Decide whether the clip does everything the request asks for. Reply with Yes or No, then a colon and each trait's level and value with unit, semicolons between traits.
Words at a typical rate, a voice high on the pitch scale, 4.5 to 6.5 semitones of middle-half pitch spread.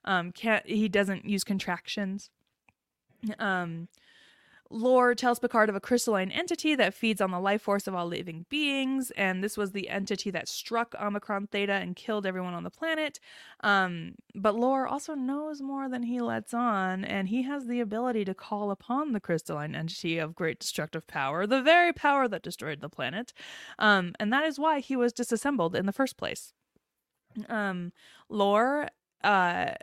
Yes: average, 175 wpm; high, 210 Hz; average, 4.9 semitones